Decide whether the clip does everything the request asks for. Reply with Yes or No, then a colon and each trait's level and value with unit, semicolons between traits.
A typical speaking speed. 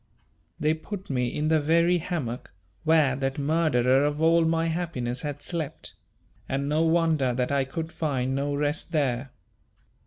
Yes: average, 155 wpm